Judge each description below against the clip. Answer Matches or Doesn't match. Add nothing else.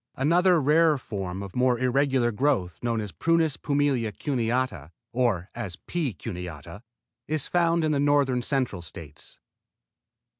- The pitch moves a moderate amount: Doesn't match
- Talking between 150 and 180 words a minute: Doesn't match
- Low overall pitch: Matches